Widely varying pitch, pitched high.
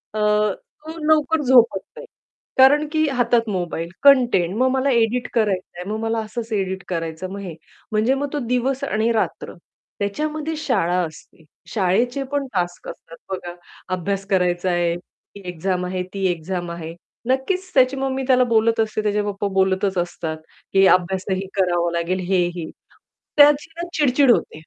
Yes: wide, 6.2 semitones; high, 210 Hz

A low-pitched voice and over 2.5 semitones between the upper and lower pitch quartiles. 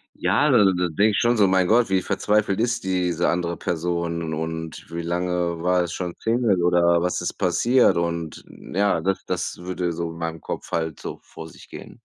No: very low, 90 Hz; narrow, 2.2 semitones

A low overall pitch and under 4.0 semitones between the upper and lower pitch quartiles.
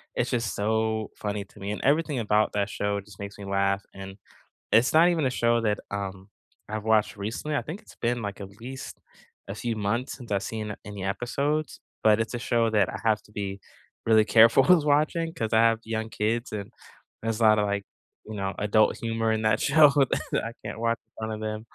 Yes: low, 110 Hz; narrow, 2.4 semitones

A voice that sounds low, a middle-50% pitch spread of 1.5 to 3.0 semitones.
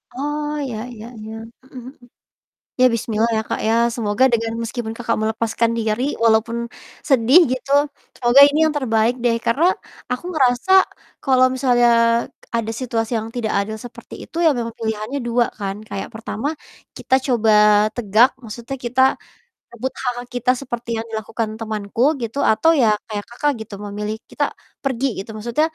No: high, 235 Hz; narrow, 2.5 semitones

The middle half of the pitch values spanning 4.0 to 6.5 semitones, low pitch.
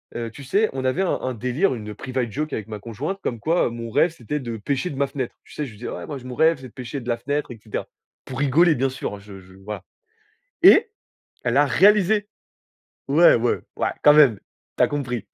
Yes: average, 4.3 semitones; low, 130 Hz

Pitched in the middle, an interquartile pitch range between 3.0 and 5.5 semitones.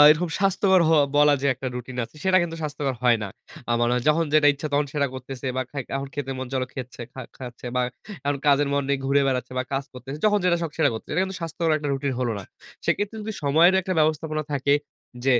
Yes: medium, 145 Hz; average, 3.5 semitones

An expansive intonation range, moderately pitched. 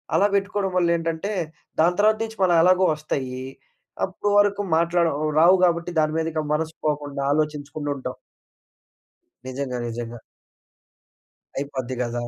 No: average, 4.5 semitones; medium, 160 Hz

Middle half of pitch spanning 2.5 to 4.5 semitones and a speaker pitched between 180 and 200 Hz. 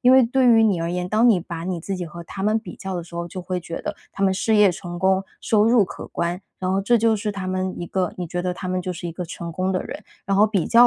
Yes: average, 3.1 semitones; medium, 185 Hz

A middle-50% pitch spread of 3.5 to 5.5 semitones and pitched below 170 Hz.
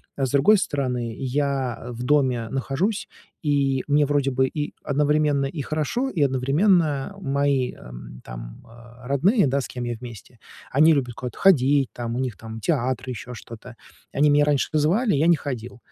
No: average, 3.1 semitones; low, 135 Hz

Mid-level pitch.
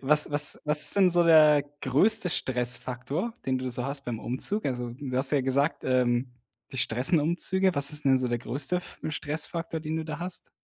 Yes: medium, 145 Hz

